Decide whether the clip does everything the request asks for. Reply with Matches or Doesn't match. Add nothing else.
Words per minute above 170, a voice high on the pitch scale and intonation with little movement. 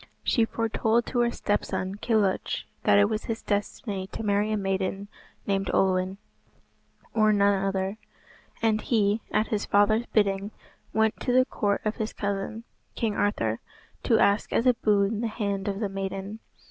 Doesn't match